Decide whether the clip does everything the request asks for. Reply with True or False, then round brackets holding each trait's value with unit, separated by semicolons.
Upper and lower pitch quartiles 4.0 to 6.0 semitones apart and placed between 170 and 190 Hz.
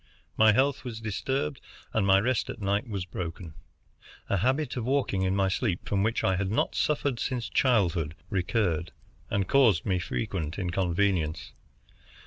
False (4.7 semitones; 100 Hz)